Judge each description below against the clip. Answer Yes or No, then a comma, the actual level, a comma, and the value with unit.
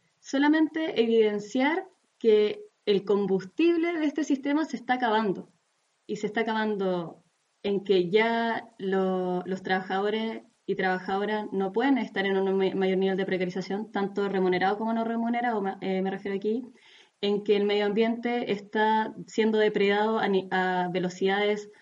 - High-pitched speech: Yes, high, 205 Hz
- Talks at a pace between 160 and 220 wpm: No, average, 145 wpm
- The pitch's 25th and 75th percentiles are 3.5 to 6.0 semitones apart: No, average, 3.1 semitones